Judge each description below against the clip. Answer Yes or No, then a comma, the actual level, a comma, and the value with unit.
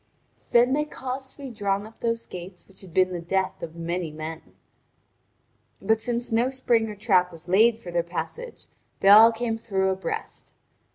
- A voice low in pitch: No, high, 205 Hz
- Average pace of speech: Yes, average, 180 wpm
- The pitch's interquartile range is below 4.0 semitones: No, average, 4.6 semitones